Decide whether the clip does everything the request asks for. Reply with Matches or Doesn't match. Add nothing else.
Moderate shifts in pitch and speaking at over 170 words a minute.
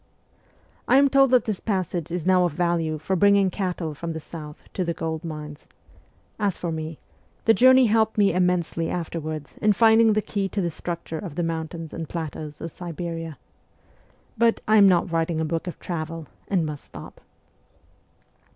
Matches